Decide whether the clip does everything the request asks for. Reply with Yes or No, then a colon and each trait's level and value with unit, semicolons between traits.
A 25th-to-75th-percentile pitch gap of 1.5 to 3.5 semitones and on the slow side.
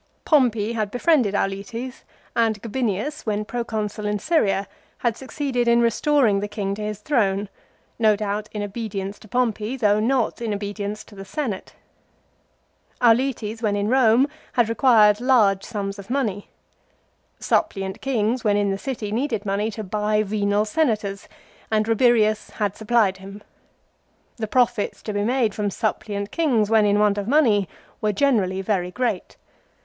No: average, 2.8 semitones; average, 155 wpm